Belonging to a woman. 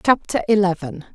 Yes: female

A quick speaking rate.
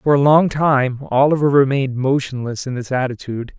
No: average, 170 wpm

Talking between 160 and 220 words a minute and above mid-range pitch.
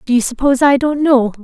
No: fast, 250 wpm; very high, 260 Hz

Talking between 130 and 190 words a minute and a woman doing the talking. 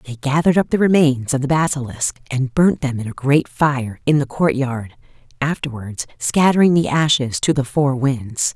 Yes: average, 180 wpm; female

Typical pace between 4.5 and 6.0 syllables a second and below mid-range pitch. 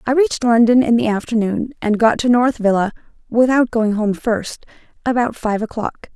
No: 5.0 syllables/s; high, 230 Hz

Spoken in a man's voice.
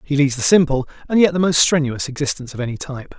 Yes: male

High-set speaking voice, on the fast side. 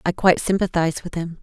No: medium, 170 Hz; fast, 210 wpm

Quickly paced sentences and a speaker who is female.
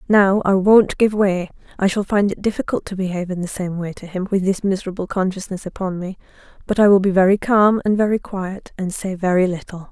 Yes: fast, 225 wpm; female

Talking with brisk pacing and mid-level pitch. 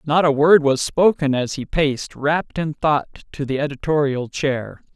No: average, 180 wpm; medium, 145 Hz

